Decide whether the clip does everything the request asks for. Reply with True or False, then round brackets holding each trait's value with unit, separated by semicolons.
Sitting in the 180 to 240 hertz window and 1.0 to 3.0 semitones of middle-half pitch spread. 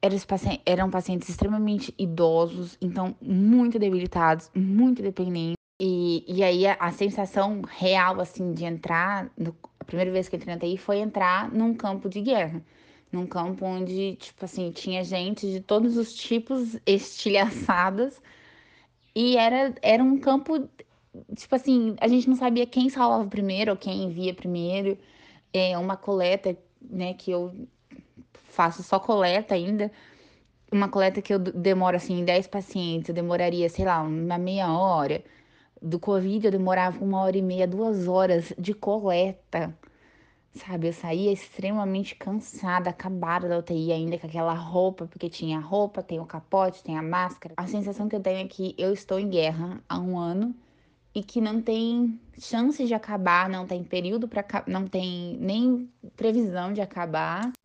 True (190 Hz; 2.7 semitones)